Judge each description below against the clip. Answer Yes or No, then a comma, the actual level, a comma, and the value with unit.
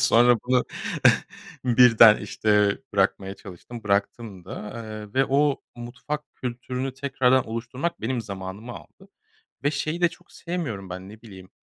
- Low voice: Yes, low, 120 Hz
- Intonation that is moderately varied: Yes, average, 4.2 semitones